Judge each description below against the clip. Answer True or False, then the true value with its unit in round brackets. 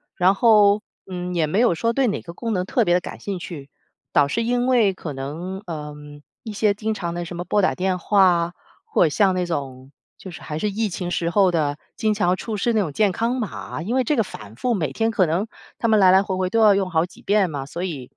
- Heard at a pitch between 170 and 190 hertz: True (185 Hz)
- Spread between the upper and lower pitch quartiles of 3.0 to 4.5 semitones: True (4.0 semitones)